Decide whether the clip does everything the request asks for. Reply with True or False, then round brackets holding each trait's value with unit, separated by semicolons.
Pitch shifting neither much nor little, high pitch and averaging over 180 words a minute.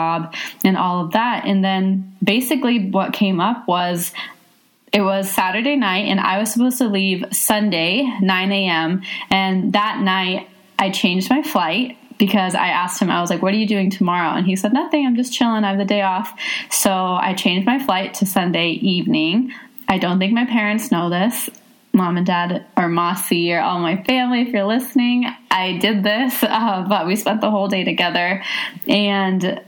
True (4.0 semitones; 200 Hz; 190 wpm)